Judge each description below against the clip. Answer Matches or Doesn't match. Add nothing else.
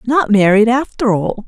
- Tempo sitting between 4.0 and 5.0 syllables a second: Matches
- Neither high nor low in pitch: Doesn't match